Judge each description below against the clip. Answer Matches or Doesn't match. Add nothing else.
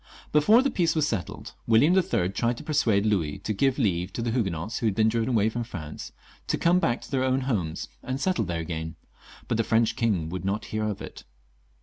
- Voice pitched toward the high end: Doesn't match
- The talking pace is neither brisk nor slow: Doesn't match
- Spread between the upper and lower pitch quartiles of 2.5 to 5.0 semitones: Doesn't match